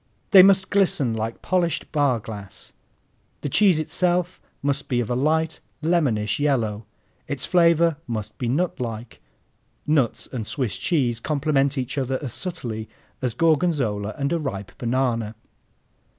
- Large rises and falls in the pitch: Yes, wide, 5.8 semitones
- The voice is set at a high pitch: No, low, 135 Hz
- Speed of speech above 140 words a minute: No, slow, 135 wpm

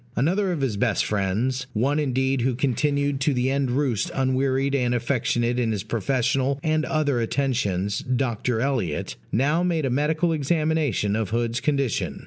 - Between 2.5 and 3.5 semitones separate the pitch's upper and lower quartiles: Yes, average, 3.2 semitones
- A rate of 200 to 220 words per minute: No, average, 155 wpm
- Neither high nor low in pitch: No, low, 130 Hz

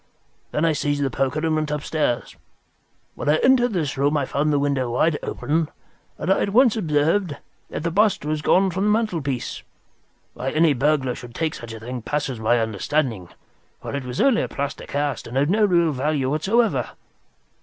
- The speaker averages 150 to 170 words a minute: No, average, 190 wpm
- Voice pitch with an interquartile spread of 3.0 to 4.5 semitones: Yes, average, 3.9 semitones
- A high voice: No, medium, 150 Hz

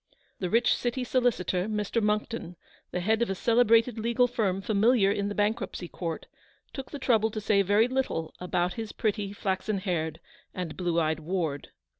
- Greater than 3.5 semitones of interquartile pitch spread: Yes, average, 4.1 semitones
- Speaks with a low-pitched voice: No, high, 205 Hz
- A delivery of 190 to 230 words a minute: No, average, 175 wpm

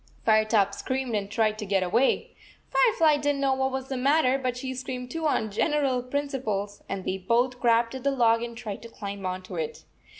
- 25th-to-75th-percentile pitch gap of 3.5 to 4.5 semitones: Yes, average, 3.8 semitones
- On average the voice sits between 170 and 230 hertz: No, very high, 250 Hz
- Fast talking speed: Yes, fast, 220 wpm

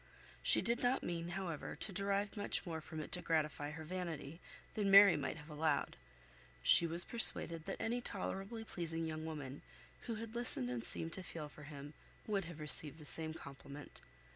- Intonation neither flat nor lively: Yes, average, 4.6 semitones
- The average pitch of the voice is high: No, medium, 165 Hz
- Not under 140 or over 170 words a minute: No, average, 185 wpm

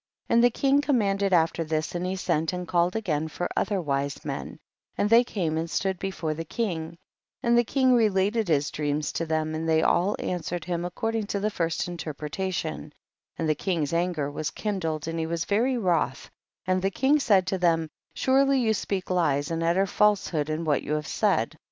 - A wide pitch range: No, average, 4.2 semitones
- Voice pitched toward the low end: No, medium, 175 Hz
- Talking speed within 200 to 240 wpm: Yes, fast, 205 wpm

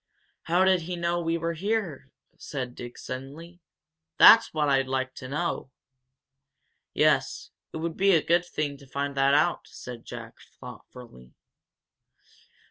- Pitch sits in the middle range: Yes, medium, 150 Hz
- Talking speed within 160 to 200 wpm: No, average, 140 wpm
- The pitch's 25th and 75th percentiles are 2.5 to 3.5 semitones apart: No, average, 4.3 semitones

